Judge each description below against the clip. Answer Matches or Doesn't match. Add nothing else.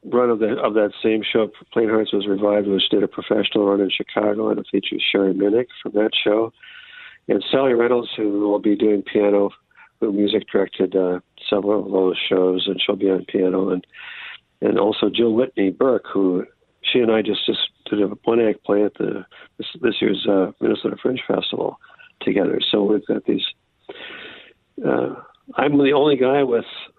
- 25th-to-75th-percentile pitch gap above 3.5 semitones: Doesn't match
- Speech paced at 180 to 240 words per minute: Matches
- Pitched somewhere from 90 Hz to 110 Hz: Matches